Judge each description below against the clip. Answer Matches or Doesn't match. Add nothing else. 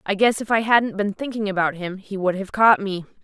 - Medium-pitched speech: Doesn't match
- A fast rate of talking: Matches